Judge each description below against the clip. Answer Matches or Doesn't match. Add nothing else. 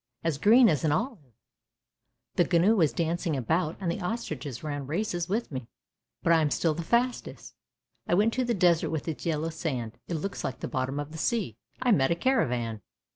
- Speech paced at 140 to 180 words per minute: Doesn't match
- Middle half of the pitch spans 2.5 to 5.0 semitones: Doesn't match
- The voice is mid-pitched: Matches